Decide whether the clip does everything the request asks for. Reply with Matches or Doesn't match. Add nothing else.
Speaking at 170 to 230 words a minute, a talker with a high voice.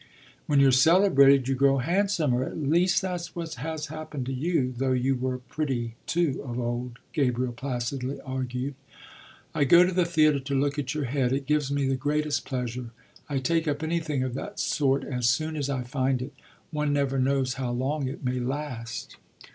Doesn't match